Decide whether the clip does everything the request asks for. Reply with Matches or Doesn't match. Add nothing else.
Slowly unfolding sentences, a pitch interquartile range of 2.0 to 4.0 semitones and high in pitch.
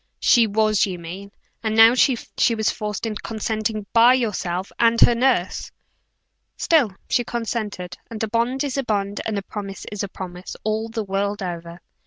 Doesn't match